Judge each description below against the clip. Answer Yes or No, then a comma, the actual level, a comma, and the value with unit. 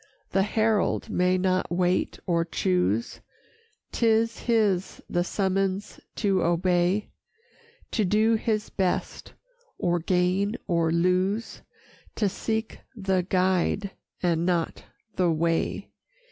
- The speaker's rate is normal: No, slow, 105 wpm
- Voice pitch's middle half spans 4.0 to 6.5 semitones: No, average, 2.9 semitones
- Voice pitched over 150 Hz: Yes, medium, 185 Hz